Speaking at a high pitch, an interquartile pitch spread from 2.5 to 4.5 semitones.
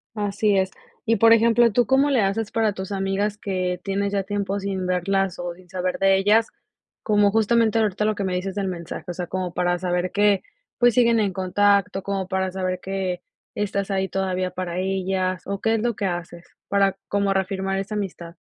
No: high, 195 Hz; narrow, 1.9 semitones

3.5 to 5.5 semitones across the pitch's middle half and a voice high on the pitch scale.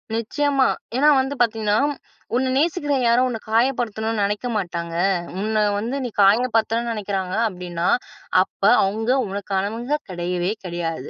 Yes: average, 4.3 semitones; high, 220 Hz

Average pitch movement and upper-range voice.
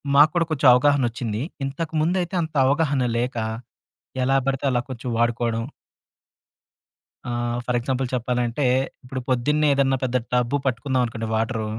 No: average, 3.1 semitones; low, 130 Hz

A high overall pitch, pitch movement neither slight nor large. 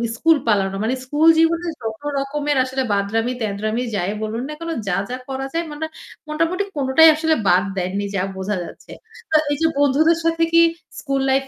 No: very high, 265 Hz; wide, 6.5 semitones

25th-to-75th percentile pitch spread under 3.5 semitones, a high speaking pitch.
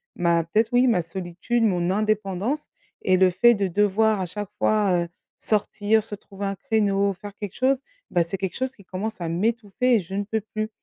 Yes: average, 2.9 semitones; high, 205 Hz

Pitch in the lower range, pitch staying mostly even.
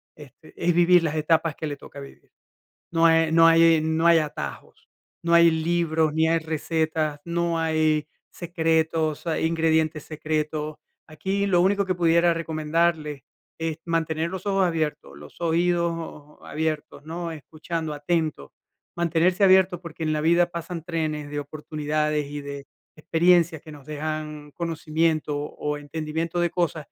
No: medium, 160 Hz; narrow, 1.7 semitones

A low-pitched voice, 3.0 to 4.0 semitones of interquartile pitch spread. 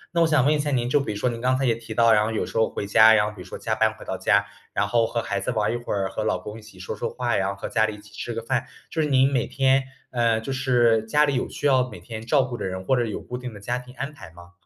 Yes: low, 115 Hz; average, 3.5 semitones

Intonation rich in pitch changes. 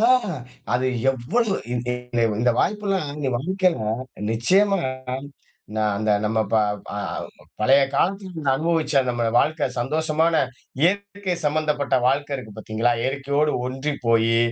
Yes: wide, 5.8 semitones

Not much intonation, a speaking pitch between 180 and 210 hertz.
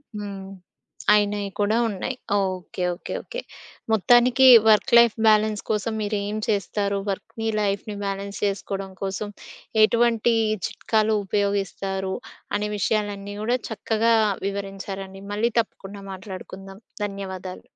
Yes: narrow, 1.8 semitones; high, 205 Hz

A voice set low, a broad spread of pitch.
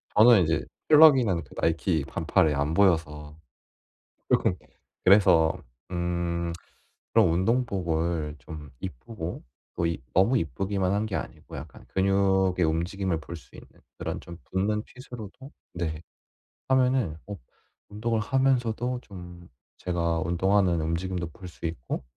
No: very low, 90 Hz; average, 4.0 semitones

